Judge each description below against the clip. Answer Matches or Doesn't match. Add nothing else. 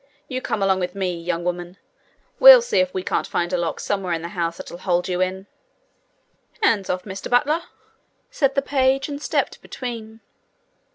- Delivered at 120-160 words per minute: Doesn't match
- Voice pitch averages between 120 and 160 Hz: Doesn't match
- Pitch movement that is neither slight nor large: Doesn't match